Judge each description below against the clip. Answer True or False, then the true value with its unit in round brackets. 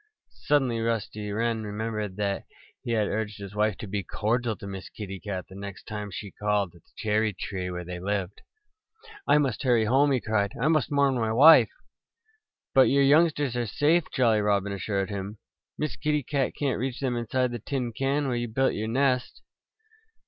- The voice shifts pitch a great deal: False (4.5 semitones)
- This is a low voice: True (110 Hz)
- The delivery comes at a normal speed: True (190 wpm)